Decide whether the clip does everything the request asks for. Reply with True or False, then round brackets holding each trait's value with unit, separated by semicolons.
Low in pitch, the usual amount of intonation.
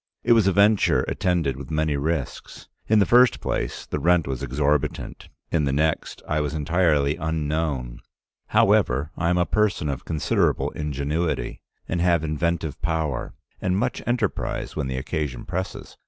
True (80 Hz; 3.7 semitones)